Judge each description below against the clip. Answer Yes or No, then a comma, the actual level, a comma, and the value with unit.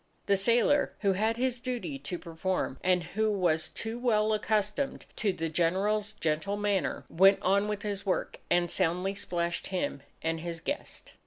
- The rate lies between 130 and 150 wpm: No, average, 165 wpm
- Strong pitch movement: No, average, 3.6 semitones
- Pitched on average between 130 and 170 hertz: No, high, 200 Hz